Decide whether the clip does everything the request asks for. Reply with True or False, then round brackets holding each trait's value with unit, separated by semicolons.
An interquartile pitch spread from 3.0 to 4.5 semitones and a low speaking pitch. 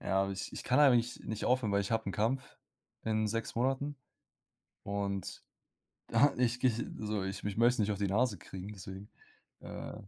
True (3.7 semitones; 110 Hz)